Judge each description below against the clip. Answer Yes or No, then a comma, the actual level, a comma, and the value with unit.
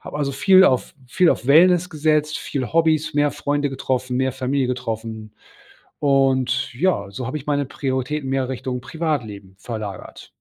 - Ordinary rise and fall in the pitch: Yes, average, 3.2 semitones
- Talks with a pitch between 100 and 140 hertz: Yes, low, 135 Hz